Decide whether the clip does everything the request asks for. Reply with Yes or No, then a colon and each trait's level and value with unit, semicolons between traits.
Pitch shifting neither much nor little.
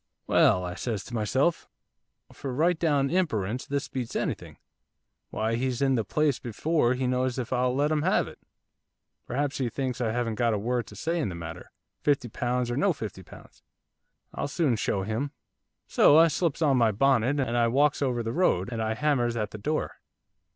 Yes: average, 4.0 semitones